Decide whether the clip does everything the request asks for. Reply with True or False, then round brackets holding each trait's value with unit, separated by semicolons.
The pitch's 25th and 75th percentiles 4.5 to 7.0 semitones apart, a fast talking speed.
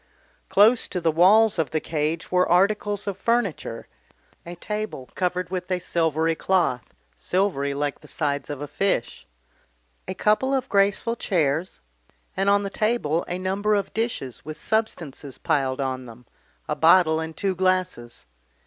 False (5.1 semitones; 155 wpm)